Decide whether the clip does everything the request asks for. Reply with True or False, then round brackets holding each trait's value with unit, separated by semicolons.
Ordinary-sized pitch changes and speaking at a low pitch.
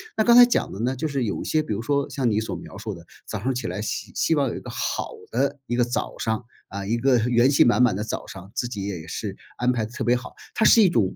True (4.1 semitones; 120 Hz)